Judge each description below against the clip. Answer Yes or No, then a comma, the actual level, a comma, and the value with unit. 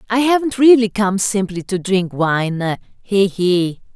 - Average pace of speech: Yes, average, 150 wpm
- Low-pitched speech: No, high, 200 Hz